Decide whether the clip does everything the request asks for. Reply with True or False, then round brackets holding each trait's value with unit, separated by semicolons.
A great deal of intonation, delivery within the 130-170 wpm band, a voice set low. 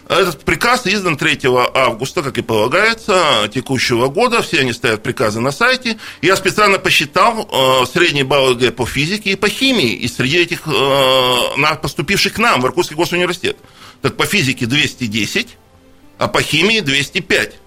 False (6.7 semitones; 145 wpm; 155 Hz)